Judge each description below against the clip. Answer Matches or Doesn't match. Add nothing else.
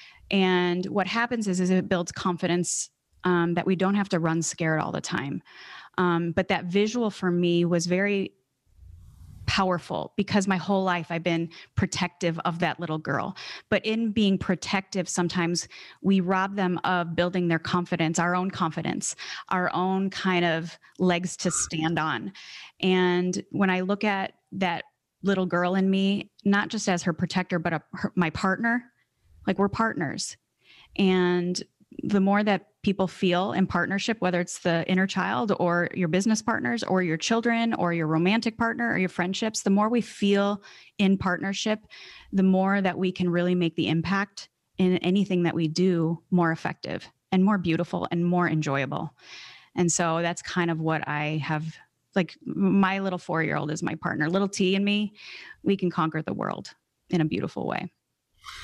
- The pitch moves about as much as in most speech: Doesn't match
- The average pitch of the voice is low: Doesn't match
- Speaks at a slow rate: Doesn't match